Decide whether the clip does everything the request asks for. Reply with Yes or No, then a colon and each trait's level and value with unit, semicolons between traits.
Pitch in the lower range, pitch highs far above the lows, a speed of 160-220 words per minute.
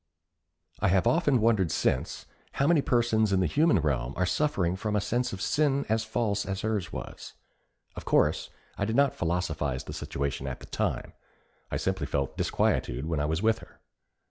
Yes: low, 100 Hz; wide, 6.0 semitones; average, 185 wpm